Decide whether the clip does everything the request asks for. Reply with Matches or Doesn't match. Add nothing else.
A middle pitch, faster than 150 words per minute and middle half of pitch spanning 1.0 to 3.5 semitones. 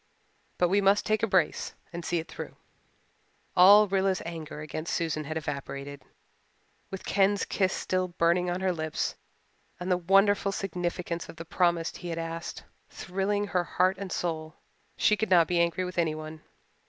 Matches